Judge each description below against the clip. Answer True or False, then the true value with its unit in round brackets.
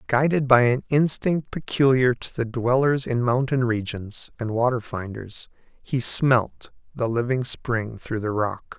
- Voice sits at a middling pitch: False (125 Hz)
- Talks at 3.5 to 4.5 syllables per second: True (4.0 syllables/s)